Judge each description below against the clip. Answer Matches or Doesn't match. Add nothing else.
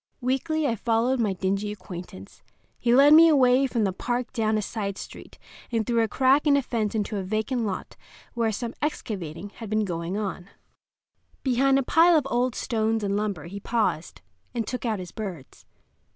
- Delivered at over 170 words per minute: Matches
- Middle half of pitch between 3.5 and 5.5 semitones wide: Matches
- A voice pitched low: Doesn't match